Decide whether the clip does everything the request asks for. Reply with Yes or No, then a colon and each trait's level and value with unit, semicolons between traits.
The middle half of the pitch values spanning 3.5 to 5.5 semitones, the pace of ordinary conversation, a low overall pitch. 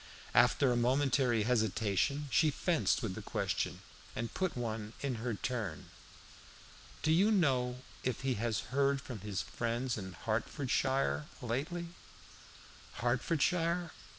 No: average, 4.0 semitones; slow, 125 wpm; low, 125 Hz